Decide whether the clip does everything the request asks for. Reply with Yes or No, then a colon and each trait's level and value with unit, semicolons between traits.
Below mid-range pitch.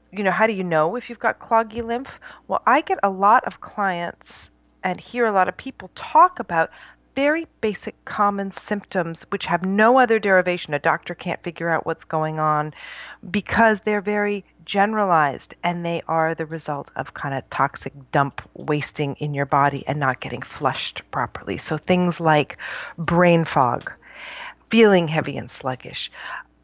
No: medium, 185 Hz